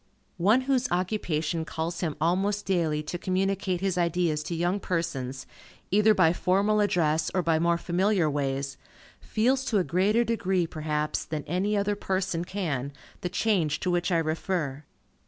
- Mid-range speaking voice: Yes, medium, 175 Hz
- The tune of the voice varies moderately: Yes, average, 3.8 semitones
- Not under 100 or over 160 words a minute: Yes, average, 155 wpm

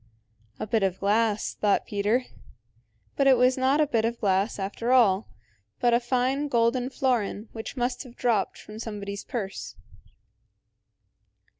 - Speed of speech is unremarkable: Yes, average, 145 wpm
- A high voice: Yes, high, 230 Hz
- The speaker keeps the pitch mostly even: No, average, 3.4 semitones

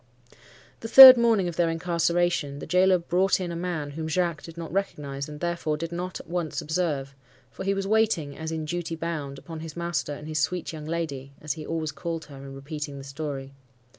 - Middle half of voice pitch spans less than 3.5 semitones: Yes, average, 2.9 semitones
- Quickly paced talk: Yes, fast, 210 wpm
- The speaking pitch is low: No, medium, 165 Hz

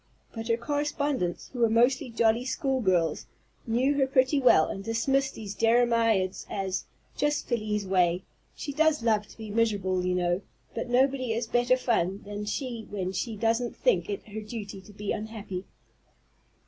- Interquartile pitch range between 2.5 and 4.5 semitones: Yes, average, 4.1 semitones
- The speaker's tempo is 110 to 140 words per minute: No, average, 165 wpm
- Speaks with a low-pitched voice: No, high, 225 Hz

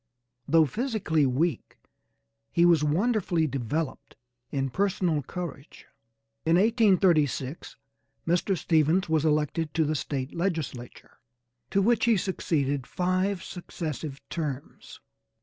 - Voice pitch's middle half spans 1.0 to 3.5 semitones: No, average, 4.2 semitones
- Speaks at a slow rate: Yes, slow, 105 wpm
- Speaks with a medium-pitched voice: Yes, medium, 160 Hz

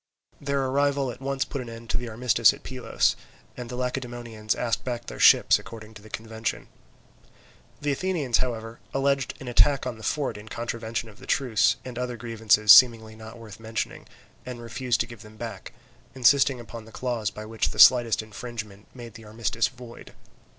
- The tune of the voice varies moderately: No, narrow, 2.3 semitones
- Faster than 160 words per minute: Yes, average, 185 wpm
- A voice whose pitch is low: Yes, low, 120 Hz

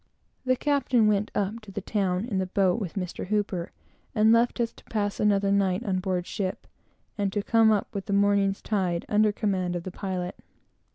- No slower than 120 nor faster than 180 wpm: No, average, 190 wpm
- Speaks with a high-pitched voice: Yes, high, 200 Hz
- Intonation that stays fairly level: Yes, narrow, 2.3 semitones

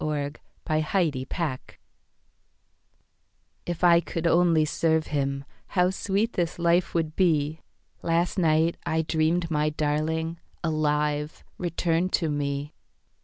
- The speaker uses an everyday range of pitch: No, narrow, 2.3 semitones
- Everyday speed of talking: No, slow, 105 wpm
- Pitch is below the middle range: No, medium, 160 Hz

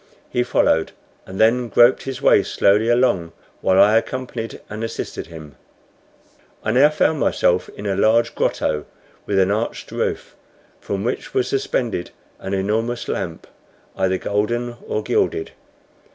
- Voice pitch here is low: Yes, low, 110 Hz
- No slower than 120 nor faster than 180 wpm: Yes, average, 140 wpm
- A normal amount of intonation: Yes, average, 3.8 semitones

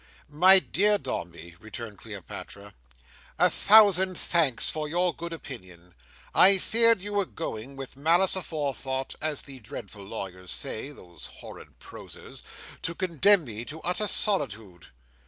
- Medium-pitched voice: Yes, medium, 145 Hz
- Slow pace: Yes, slow, 125 wpm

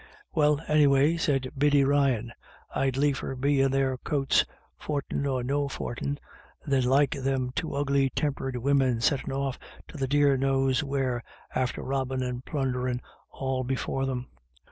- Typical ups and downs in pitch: No, narrow, 1.6 semitones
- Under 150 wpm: No, average, 160 wpm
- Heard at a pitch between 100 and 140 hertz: Yes, low, 135 Hz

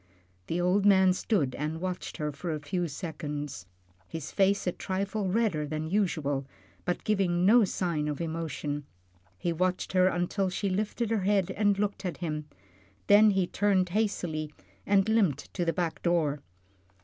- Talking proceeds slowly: No, average, 165 wpm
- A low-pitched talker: No, medium, 180 Hz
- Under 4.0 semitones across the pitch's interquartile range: No, average, 4.3 semitones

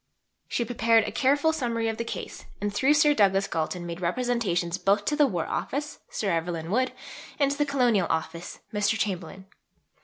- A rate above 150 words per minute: Yes, average, 180 wpm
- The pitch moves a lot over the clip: Yes, wide, 6.5 semitones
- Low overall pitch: No, high, 215 Hz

